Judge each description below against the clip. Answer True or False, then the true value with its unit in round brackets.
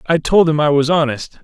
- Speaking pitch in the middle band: True (155 Hz)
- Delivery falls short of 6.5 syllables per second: True (5.3 syllables/s)